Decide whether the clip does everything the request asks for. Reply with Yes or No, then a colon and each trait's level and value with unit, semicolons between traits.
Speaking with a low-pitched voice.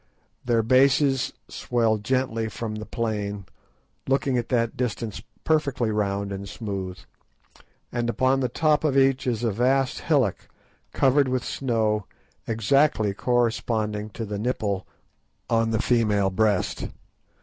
Yes: low, 115 Hz